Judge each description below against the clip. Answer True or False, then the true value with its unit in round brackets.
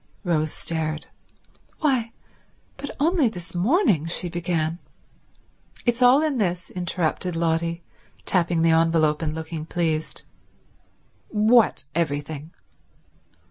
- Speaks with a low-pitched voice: False (170 Hz)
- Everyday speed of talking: False (100 wpm)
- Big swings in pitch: False (5.0 semitones)